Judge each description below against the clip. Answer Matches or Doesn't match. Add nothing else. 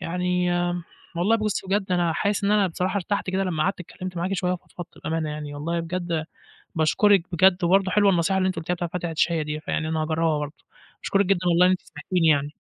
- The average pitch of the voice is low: Doesn't match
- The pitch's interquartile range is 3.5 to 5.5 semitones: Doesn't match